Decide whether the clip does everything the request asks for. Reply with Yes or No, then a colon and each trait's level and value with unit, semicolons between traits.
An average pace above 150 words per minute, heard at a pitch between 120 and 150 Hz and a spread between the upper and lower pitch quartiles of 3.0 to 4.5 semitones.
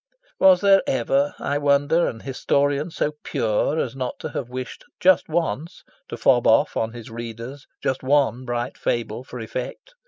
Yes: average, 165 wpm; low, 135 Hz; average, 3.5 semitones